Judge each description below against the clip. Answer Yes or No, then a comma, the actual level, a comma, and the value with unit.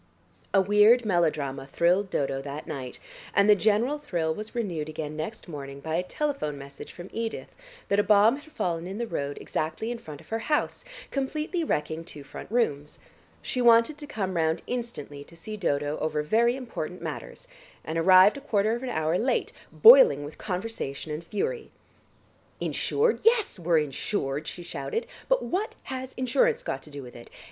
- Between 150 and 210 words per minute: Yes, average, 180 wpm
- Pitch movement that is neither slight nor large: No, wide, 7.8 semitones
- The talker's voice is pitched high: Yes, high, 195 Hz